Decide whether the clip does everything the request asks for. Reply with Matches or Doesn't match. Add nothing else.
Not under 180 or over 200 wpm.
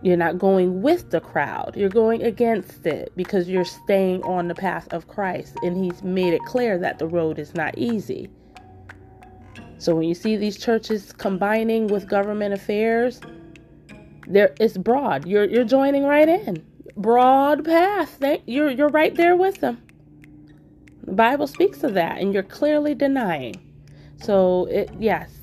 Doesn't match